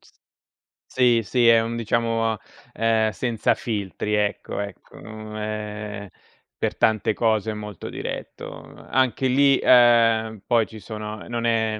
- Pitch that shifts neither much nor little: No, narrow, 1.7 semitones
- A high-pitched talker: No, low, 110 Hz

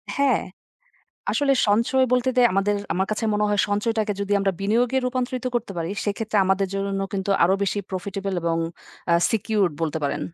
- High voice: Yes, high, 205 Hz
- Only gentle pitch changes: No, average, 3.1 semitones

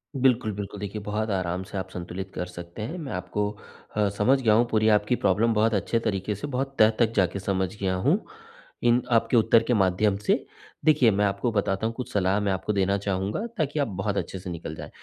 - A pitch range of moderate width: Yes, average, 3.1 semitones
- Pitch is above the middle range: No, low, 105 Hz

